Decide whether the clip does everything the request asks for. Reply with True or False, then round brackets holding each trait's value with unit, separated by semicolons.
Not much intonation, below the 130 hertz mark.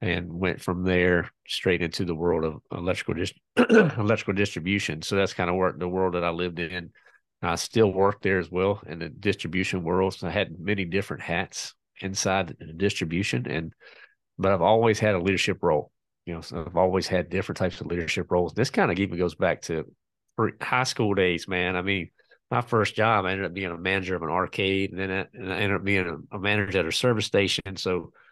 True (2.1 semitones; 95 Hz)